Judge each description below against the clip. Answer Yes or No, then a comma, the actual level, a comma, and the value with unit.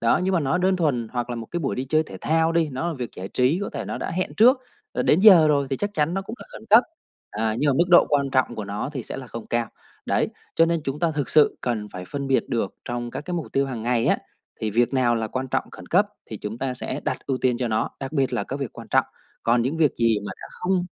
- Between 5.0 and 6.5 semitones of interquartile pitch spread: Yes, wide, 5.5 semitones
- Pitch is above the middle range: No, low, 135 Hz